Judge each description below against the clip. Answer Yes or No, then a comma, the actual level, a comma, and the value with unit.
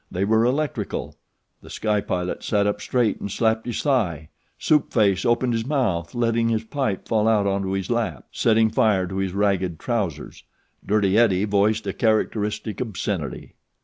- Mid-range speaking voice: No, low, 105 Hz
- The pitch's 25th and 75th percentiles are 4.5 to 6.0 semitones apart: No, average, 3.0 semitones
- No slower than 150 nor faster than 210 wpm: Yes, average, 165 wpm